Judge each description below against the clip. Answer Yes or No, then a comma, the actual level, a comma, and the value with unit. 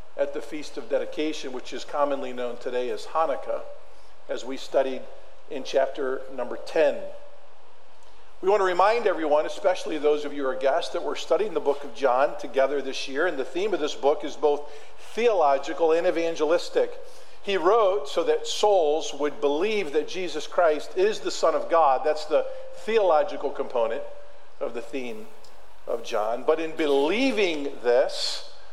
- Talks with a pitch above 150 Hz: Yes, medium, 185 Hz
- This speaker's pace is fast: No, average, 165 wpm